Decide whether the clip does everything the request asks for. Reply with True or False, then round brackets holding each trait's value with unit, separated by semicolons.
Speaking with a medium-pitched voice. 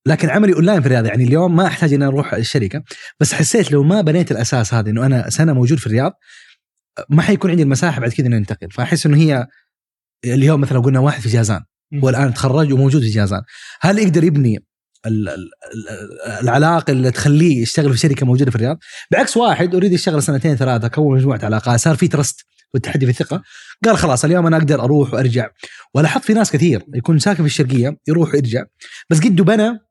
True (145 Hz)